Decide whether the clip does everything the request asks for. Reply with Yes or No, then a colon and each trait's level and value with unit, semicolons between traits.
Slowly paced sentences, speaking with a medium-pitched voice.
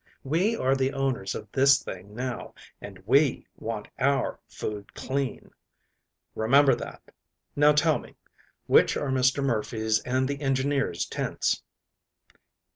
No: slow, 125 wpm; low, 130 Hz